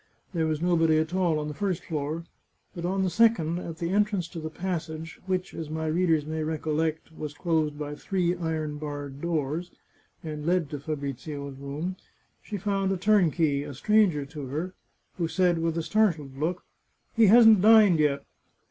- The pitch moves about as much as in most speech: Yes, average, 3.2 semitones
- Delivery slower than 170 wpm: No, average, 185 wpm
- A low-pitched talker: No, medium, 160 Hz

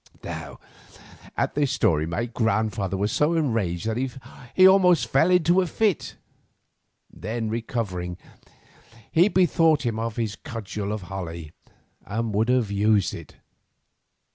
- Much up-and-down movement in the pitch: Yes, wide, 6.6 semitones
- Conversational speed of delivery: No, slow, 130 wpm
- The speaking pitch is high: No, low, 115 Hz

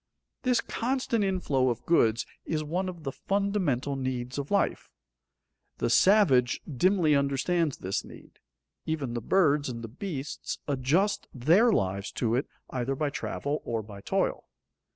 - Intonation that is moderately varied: No, wide, 6.7 semitones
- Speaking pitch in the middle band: Yes, medium, 145 Hz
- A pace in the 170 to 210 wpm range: No, average, 145 wpm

